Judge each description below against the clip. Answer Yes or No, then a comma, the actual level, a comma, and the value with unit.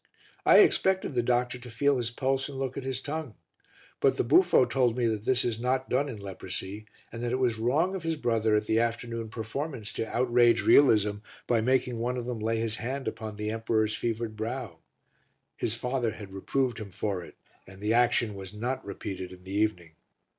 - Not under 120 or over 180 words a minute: No, fast, 205 wpm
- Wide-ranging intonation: No, average, 3.0 semitones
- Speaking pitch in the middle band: No, low, 115 Hz